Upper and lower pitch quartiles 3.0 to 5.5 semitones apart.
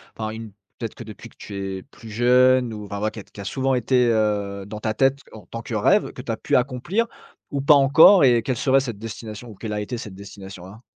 Yes: average, 3.5 semitones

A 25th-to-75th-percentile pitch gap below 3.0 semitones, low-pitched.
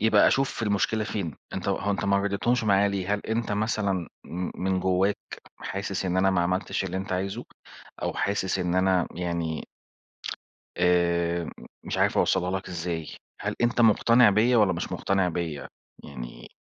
Yes: narrow, 2.5 semitones; very low, 95 Hz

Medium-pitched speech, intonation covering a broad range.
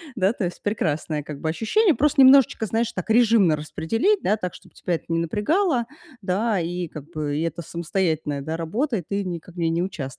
Yes: medium, 180 Hz; wide, 5.8 semitones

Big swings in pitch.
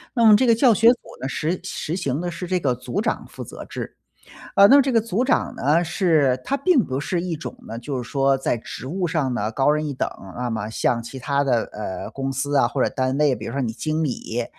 Yes: wide, 6.1 semitones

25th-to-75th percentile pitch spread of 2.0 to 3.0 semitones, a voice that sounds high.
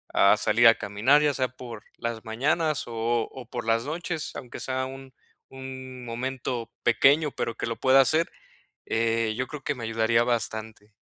No: narrow, 2.6 semitones; low, 125 Hz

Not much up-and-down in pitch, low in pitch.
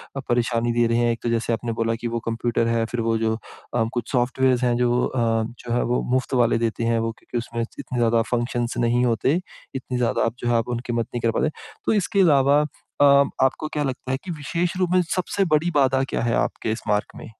Yes: narrow, 2.2 semitones; low, 120 Hz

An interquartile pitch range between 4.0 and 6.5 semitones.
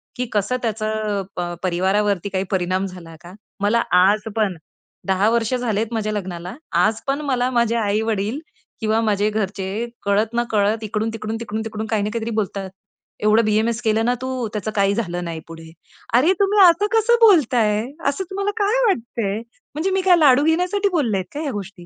No: average, 3.6 semitones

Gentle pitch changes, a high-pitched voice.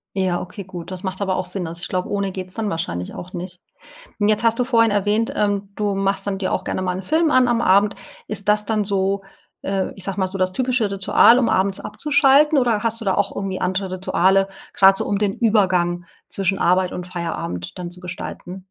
Yes: narrow, 2.3 semitones; high, 195 Hz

